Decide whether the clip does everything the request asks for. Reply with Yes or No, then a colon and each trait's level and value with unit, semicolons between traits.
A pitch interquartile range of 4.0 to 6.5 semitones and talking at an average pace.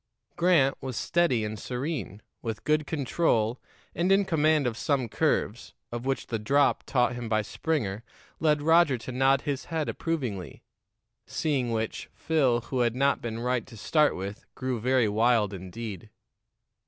Yes: average, 5.0 semitones; average, 155 wpm